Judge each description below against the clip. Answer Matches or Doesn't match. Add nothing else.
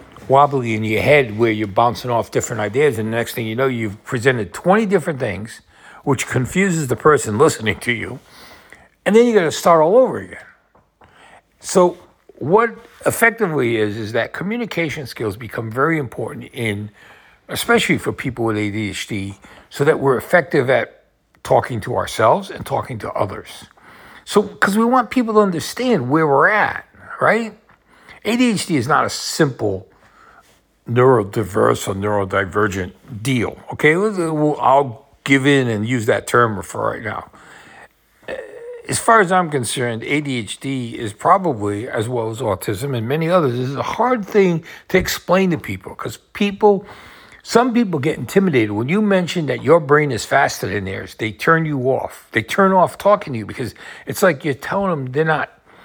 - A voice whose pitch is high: Doesn't match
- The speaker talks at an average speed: Matches